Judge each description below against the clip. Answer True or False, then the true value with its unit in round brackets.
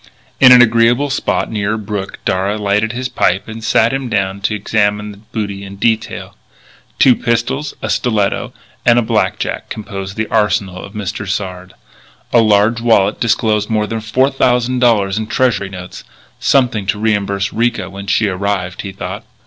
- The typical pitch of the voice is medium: False (105 Hz)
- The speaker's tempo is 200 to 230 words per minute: False (170 wpm)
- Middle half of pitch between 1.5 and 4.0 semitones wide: True (2.8 semitones)